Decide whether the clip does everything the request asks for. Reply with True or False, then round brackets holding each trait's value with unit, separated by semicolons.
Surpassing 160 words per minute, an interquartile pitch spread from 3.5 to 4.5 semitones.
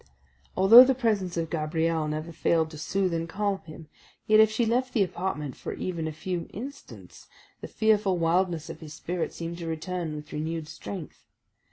True (180 wpm; 3.8 semitones)